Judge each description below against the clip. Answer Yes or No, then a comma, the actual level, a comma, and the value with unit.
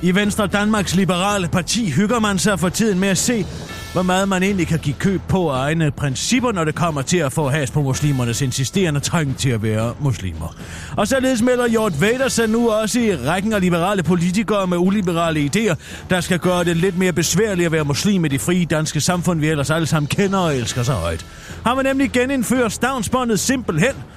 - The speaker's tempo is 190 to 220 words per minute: Yes, average, 210 wpm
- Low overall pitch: No, medium, 180 Hz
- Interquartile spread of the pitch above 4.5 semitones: Yes, wide, 5.6 semitones